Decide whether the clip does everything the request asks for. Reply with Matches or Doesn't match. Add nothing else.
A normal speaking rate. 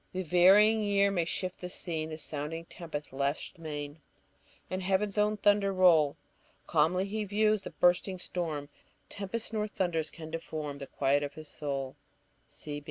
Matches